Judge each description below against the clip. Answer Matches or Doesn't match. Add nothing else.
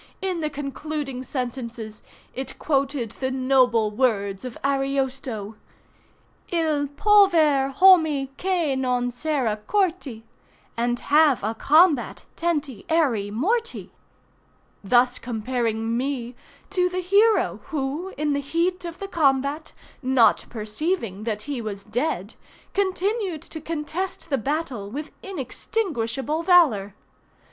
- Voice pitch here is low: Doesn't match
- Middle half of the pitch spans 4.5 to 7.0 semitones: Matches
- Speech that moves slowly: Matches